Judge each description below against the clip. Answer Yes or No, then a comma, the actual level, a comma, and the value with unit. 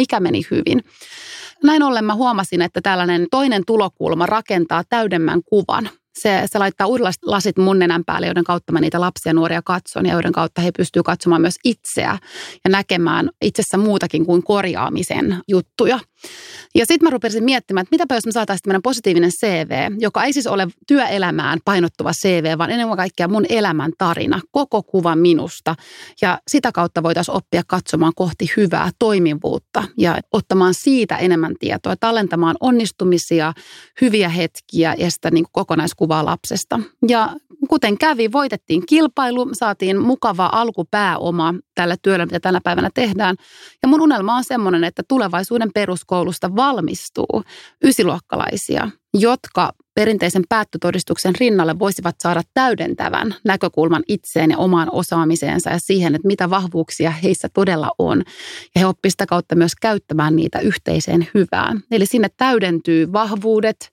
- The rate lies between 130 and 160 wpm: Yes, average, 145 wpm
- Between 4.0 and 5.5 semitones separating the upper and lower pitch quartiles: Yes, average, 4.7 semitones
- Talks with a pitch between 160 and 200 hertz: Yes, high, 190 Hz